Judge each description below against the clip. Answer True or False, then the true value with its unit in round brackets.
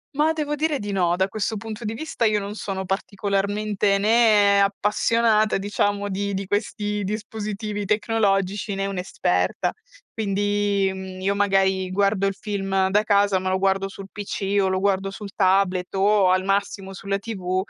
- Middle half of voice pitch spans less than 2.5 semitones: True (1.4 semitones)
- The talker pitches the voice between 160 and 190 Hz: False (200 Hz)